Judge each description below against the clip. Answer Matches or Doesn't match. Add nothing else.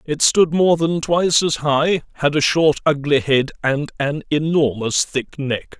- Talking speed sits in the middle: Matches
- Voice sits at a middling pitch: Matches